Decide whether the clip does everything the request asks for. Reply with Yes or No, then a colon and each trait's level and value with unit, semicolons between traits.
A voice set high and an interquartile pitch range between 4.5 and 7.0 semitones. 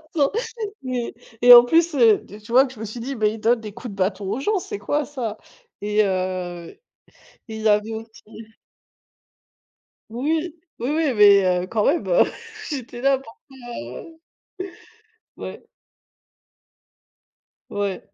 Yes: high, 225 Hz; average, 4.8 semitones